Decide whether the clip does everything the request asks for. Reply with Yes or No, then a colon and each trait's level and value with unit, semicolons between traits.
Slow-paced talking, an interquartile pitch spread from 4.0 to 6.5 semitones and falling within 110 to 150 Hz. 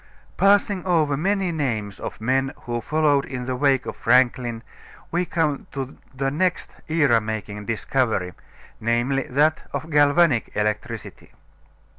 Yes: slow, 130 wpm; average, 5.0 semitones; low, 135 Hz